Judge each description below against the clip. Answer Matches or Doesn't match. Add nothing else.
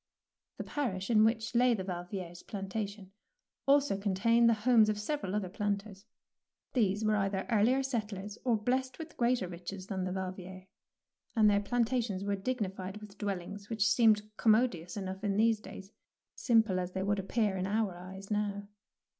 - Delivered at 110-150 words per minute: Doesn't match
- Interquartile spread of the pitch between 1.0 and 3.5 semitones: Matches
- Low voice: Doesn't match